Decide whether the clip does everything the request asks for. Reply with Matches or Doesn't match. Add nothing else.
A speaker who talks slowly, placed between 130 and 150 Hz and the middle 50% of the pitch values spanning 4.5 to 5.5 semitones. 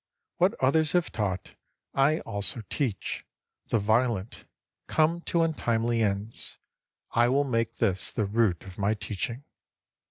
Doesn't match